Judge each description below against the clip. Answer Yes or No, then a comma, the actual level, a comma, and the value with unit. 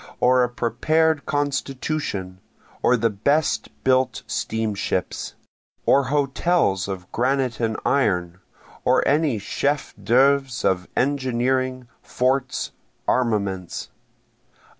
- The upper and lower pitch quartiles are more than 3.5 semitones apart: Yes, average, 4.4 semitones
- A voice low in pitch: Yes, low, 125 Hz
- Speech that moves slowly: Yes, slow, 95 wpm